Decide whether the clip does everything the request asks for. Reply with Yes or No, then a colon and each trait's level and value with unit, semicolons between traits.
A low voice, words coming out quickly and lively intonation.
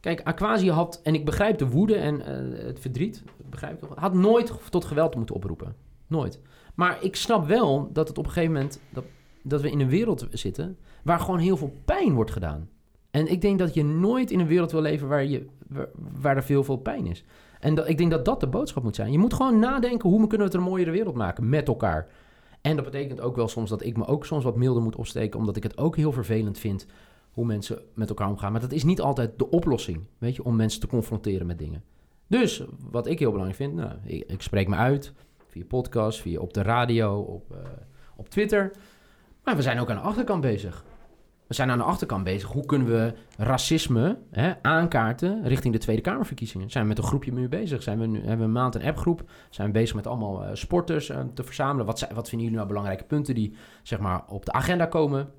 Yes: low, 130 Hz; fast, 240 wpm; wide, 6.6 semitones